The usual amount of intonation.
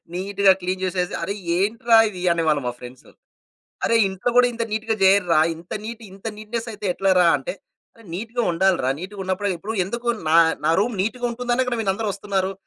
Yes: average, 3.7 semitones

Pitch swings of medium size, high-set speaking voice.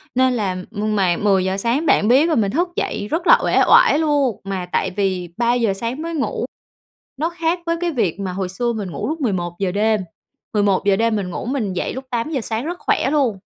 No: wide, 6.7 semitones; high, 220 Hz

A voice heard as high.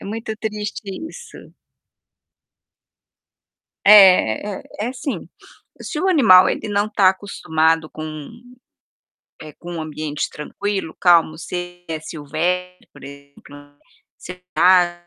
No: medium, 180 Hz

